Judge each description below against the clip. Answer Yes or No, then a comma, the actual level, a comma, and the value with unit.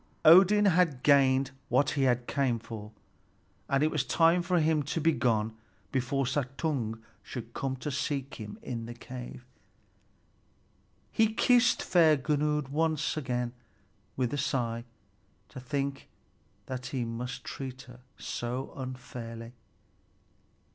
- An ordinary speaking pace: No, slow, 125 wpm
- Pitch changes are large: No, average, 3.6 semitones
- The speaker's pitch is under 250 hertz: Yes, low, 135 Hz